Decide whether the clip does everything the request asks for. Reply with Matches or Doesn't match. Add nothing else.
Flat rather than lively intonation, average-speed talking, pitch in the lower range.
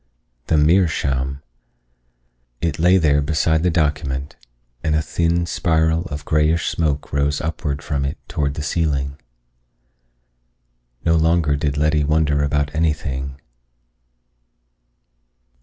Doesn't match